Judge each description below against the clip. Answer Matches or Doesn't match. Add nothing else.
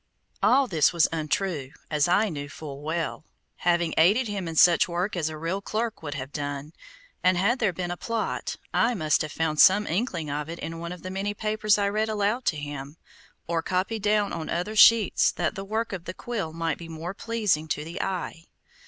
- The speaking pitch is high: Doesn't match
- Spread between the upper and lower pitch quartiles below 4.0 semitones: Doesn't match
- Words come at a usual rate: Doesn't match